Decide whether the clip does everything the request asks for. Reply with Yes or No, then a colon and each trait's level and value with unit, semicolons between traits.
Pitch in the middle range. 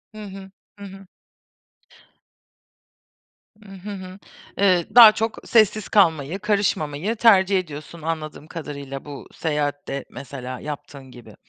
Yes: medium, 170 Hz